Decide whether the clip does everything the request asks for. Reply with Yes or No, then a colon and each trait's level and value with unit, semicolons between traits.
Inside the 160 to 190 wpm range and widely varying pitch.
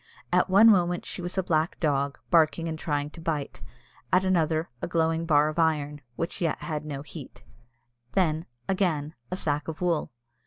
No: average, 180 wpm; average, 2.7 semitones